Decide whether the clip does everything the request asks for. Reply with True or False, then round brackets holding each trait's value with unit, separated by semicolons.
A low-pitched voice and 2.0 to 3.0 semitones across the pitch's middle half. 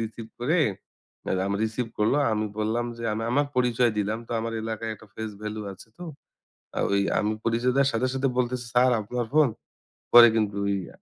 True (115 Hz; 2.5 semitones)